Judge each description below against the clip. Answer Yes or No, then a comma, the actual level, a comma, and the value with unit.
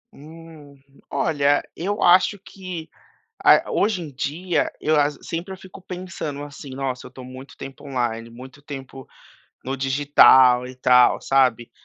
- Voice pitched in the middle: Yes, medium, 145 Hz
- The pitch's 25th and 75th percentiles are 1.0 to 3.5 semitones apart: No, average, 4.2 semitones